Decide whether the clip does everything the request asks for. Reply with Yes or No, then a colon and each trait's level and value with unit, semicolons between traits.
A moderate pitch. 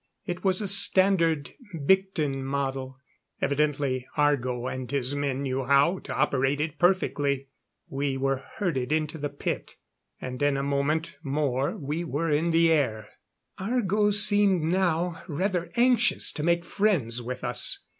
Yes: medium, 150 Hz